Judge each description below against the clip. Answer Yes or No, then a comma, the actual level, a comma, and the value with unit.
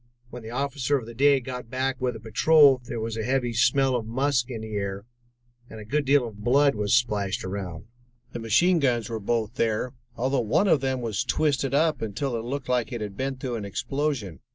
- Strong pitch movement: No, average, 3.5 semitones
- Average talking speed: No, fast, 220 wpm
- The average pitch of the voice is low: Yes, low, 120 Hz